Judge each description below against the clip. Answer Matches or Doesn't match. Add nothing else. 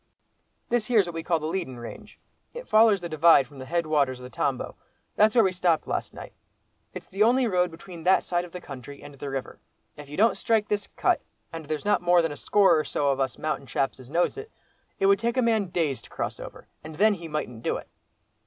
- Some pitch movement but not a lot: Doesn't match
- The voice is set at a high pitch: Doesn't match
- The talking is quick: Matches